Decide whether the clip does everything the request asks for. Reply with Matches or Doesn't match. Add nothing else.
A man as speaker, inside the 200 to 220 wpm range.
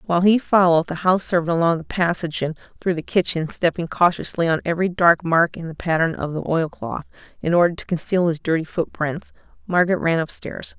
Doesn't match